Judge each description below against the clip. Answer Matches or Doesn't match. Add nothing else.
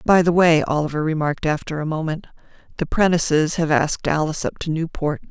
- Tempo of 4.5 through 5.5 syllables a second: Doesn't match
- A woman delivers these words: Matches